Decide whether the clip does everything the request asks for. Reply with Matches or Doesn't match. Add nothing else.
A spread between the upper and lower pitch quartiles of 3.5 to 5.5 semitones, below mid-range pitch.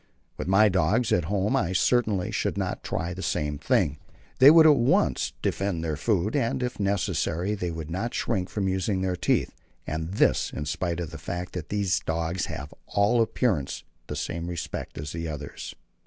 Matches